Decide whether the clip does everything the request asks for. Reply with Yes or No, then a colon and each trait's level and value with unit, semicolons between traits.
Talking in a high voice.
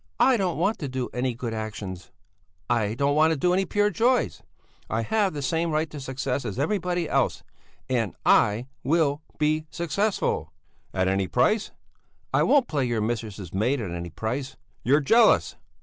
No: medium, 140 Hz